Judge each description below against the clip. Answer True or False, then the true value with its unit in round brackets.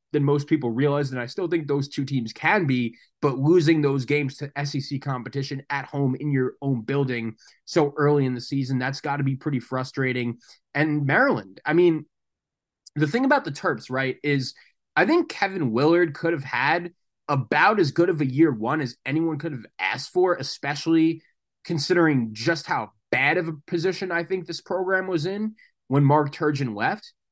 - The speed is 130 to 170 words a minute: False (190 wpm)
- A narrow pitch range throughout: False (3.8 semitones)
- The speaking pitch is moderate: True (145 Hz)